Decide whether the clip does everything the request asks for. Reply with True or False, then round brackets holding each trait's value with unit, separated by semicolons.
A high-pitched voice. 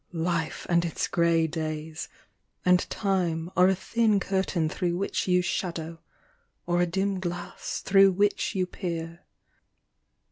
False (175 Hz)